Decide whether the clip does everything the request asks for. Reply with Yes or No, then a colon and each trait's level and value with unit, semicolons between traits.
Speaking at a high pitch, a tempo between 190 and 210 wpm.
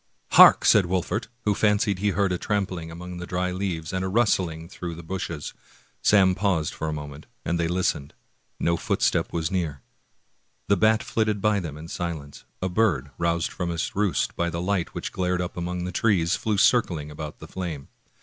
No: very low, 90 Hz; average, 195 wpm